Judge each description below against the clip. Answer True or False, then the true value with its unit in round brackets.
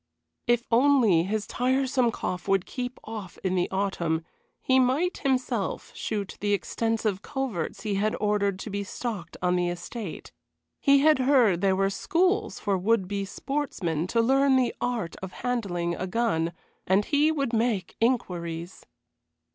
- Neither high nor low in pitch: False (215 Hz)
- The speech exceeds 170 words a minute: False (155 wpm)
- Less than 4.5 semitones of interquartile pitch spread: False (5.2 semitones)